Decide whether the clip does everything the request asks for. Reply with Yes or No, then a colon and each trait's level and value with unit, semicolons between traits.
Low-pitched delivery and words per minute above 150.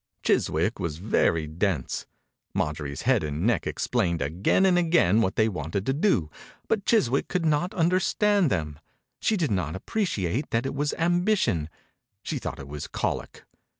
Yes: low, 110 Hz; average, 165 wpm